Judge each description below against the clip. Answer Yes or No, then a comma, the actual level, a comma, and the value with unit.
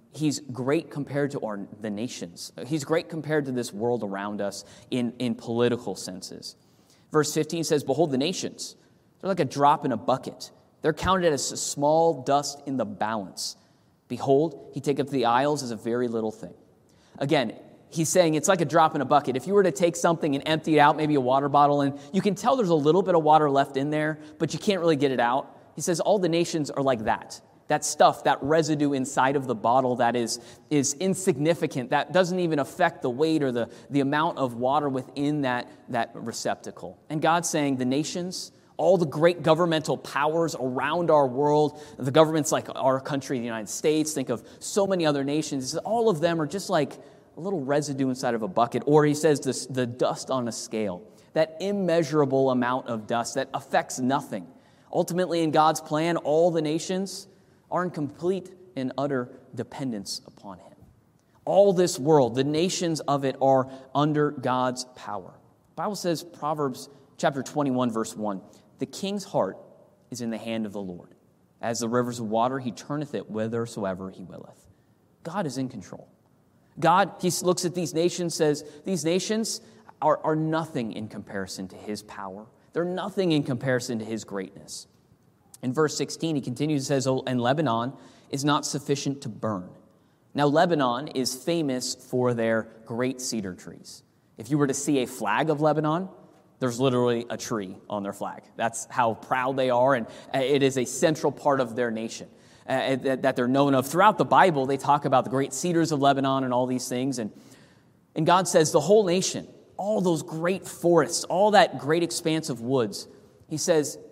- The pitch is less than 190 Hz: Yes, medium, 140 Hz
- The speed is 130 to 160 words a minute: No, average, 190 wpm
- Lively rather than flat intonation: No, average, 4.2 semitones